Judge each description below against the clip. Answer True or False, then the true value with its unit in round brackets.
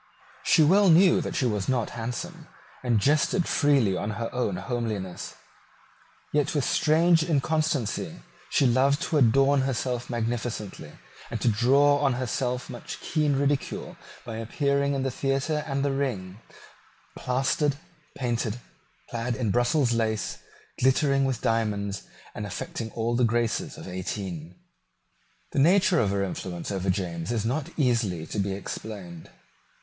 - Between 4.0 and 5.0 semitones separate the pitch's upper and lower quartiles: True (4.7 semitones)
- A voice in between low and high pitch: False (125 Hz)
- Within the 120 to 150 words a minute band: True (140 wpm)